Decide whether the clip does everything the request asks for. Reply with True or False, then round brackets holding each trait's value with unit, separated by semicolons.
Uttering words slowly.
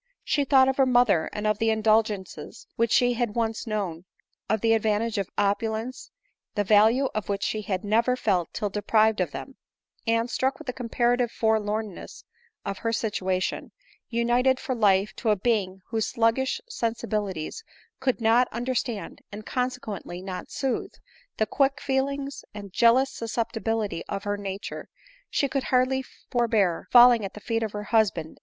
False (165 wpm)